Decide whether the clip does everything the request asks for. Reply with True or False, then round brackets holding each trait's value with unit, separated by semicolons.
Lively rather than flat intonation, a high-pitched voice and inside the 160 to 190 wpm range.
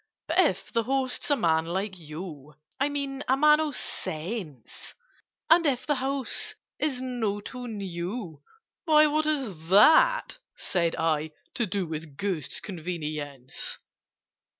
False (8.9 semitones; 205 Hz; 135 wpm)